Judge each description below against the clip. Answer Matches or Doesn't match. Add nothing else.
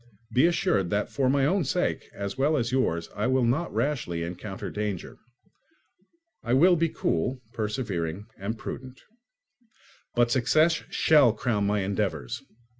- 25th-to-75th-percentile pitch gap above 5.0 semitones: Matches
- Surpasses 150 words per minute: Doesn't match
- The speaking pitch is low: Matches